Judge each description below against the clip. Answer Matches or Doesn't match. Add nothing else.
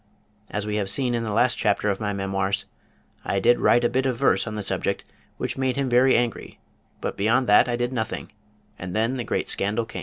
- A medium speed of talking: Doesn't match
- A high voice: Doesn't match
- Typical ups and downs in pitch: Matches